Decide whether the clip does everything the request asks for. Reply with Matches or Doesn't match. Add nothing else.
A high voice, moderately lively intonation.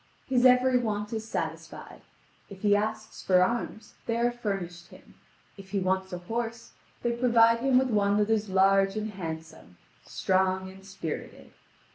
Matches